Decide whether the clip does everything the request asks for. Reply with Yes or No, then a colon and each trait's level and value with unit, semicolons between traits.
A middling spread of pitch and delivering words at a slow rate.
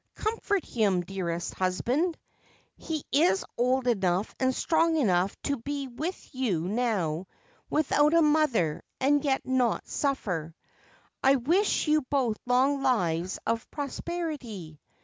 No: wide, 7.5 semitones; slow, 125 wpm